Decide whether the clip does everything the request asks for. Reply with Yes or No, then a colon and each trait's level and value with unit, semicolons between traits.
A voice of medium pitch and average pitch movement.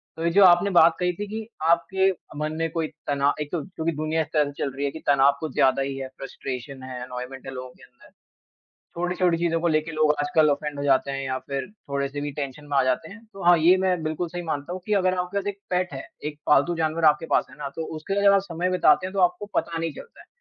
Yes: medium, 155 Hz; average, 4.2 semitones